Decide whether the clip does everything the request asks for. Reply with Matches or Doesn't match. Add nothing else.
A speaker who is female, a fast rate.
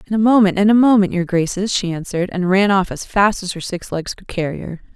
Matches